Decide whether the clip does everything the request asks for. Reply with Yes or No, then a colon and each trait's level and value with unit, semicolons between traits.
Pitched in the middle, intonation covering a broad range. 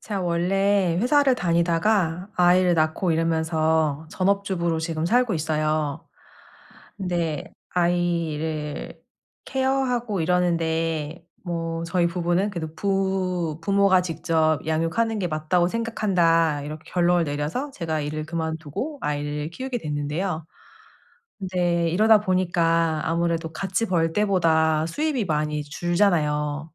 No: medium, 170 Hz; average, 3.0 semitones